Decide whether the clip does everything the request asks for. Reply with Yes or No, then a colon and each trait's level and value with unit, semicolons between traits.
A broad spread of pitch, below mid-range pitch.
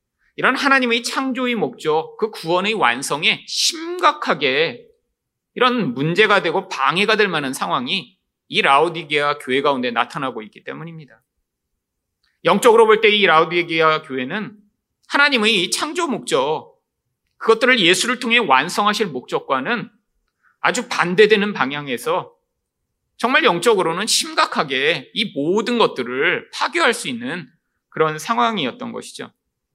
No: wide, 7.8 semitones; high, 220 Hz